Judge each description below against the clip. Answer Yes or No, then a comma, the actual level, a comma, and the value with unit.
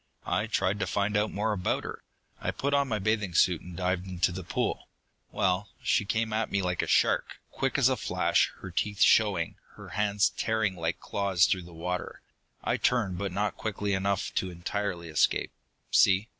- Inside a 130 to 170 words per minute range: No, average, 190 wpm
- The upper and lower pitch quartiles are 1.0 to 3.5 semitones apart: Yes, narrow, 2.6 semitones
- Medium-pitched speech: No, low, 100 Hz